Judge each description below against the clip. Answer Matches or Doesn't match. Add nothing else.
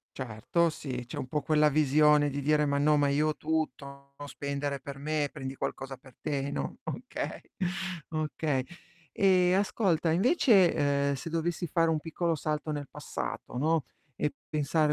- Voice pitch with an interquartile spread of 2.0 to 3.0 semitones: Matches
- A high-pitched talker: Doesn't match